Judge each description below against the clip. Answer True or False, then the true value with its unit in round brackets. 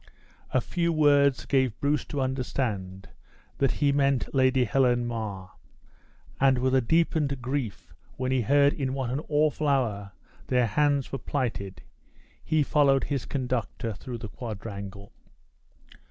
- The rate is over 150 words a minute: False (140 wpm)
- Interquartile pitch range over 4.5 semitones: False (3.3 semitones)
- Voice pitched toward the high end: False (130 Hz)